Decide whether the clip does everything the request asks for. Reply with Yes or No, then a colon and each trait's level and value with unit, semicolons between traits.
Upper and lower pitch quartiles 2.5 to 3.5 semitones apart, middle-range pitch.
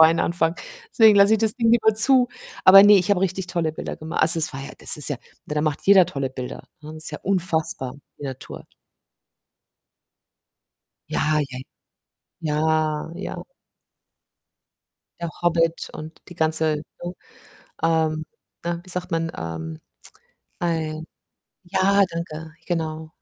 Yes: average, 2.9 semitones; medium, 165 Hz